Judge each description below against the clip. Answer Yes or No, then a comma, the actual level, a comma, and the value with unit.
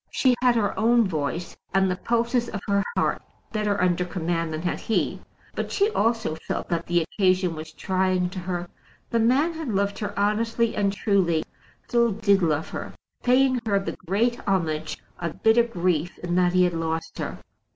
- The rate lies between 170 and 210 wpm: Yes, average, 180 wpm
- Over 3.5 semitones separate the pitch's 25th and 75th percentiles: Yes, average, 4.6 semitones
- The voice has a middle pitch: No, high, 195 Hz